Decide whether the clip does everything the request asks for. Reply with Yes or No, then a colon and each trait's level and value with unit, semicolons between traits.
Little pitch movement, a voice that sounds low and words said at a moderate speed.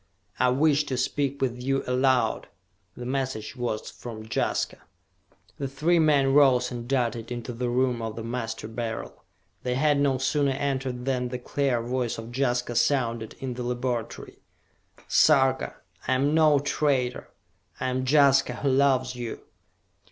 Yes: narrow, 2.1 semitones; low, 130 Hz; average, 150 wpm